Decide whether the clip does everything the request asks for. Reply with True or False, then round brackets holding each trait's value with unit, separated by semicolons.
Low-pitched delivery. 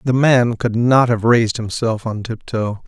True (115 Hz)